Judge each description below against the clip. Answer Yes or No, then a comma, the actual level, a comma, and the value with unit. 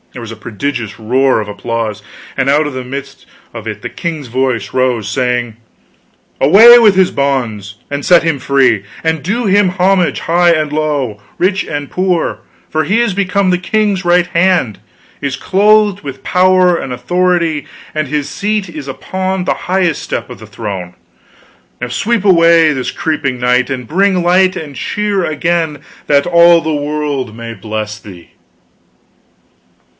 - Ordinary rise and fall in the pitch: No, wide, 6.4 semitones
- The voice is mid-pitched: Yes, medium, 150 Hz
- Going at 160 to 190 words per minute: Yes, average, 165 wpm